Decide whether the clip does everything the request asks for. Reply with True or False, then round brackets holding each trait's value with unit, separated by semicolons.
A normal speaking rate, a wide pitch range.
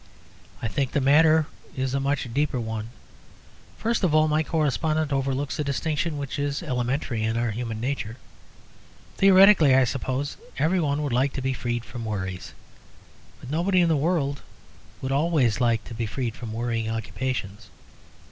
False (165 wpm; 4.3 semitones)